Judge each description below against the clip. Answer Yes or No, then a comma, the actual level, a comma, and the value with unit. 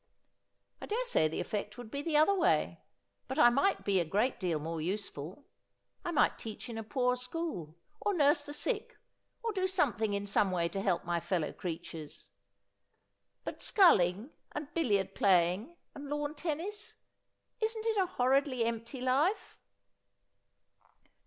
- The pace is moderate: Yes, average, 160 wpm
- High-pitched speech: Yes, very high, 250 Hz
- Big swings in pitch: Yes, wide, 8.7 semitones